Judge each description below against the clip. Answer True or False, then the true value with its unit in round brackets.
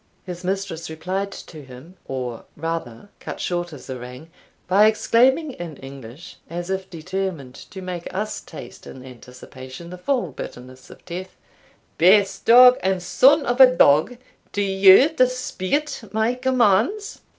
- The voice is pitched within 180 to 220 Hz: True (185 Hz)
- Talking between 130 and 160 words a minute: True (140 wpm)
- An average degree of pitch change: False (6.2 semitones)